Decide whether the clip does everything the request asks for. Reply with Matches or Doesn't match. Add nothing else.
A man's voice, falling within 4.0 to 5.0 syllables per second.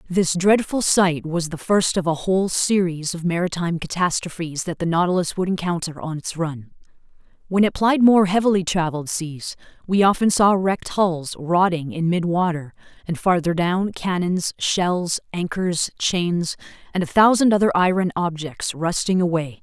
Doesn't match